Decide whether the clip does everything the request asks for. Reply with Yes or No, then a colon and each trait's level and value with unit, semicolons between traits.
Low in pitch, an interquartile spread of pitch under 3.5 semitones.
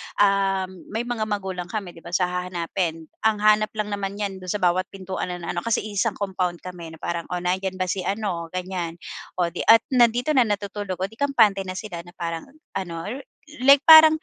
No: high, 190 Hz; average, 3.0 semitones